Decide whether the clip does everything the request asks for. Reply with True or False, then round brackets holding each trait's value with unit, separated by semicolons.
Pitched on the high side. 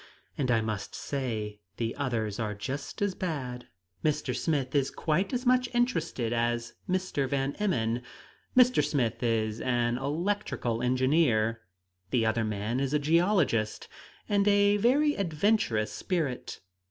False (135 Hz)